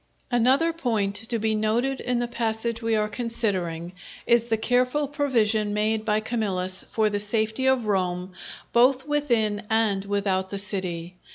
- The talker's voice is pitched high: Yes, high, 220 Hz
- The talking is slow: No, average, 155 wpm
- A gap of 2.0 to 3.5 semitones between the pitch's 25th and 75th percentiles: Yes, average, 3.0 semitones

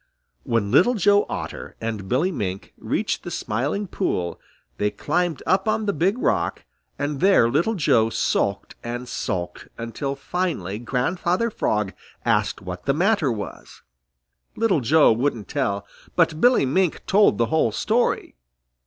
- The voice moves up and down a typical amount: No, wide, 8.8 semitones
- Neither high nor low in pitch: Yes, medium, 145 Hz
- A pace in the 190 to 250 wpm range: No, average, 145 wpm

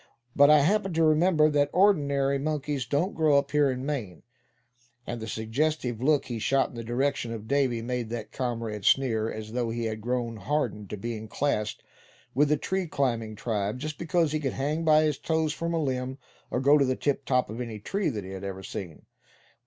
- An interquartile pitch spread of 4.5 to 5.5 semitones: Yes, average, 4.8 semitones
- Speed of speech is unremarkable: No, fast, 210 wpm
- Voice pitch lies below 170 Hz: Yes, low, 135 Hz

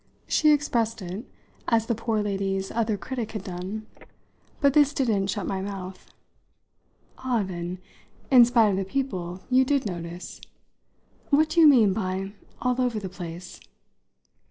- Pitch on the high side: Yes, high, 210 Hz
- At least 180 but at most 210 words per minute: No, average, 150 wpm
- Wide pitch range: No, average, 5.0 semitones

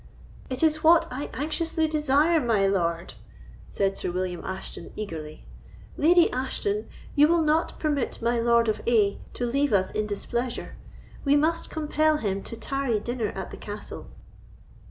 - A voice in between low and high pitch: No, very high, 250 Hz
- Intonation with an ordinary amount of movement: No, wide, 7.0 semitones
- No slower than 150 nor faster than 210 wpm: Yes, average, 155 wpm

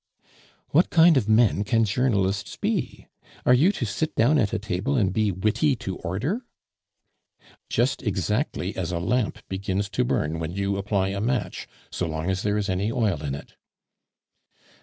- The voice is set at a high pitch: No, low, 105 Hz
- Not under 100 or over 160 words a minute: No, average, 170 wpm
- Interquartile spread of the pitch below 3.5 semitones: No, average, 4.6 semitones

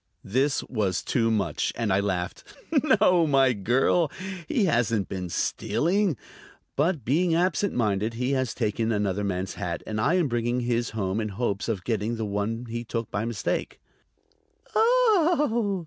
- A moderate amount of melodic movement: No, wide, 6.7 semitones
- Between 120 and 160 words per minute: Yes, average, 155 wpm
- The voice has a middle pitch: No, low, 115 Hz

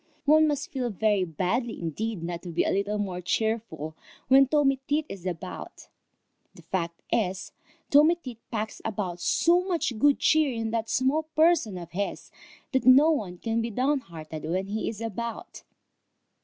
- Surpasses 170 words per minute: No, average, 165 wpm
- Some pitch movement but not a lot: No, wide, 6.7 semitones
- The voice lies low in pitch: No, high, 225 Hz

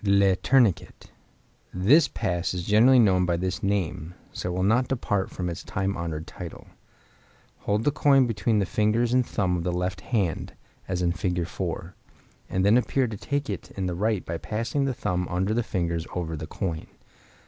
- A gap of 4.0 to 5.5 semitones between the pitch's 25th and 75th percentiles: Yes, average, 4.3 semitones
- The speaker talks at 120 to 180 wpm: No, average, 190 wpm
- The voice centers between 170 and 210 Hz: No, very low, 95 Hz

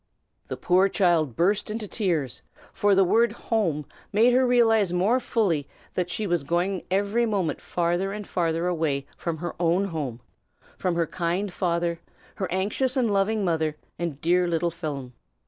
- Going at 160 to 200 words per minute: Yes, average, 165 wpm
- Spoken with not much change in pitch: No, average, 3.5 semitones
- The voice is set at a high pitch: No, medium, 180 Hz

